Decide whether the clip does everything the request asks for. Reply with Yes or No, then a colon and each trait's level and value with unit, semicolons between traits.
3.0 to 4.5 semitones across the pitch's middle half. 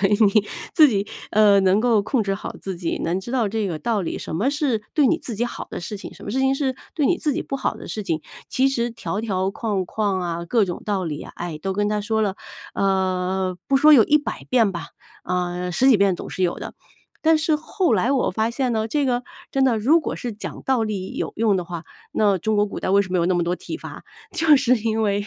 No: average, 5.1 semitones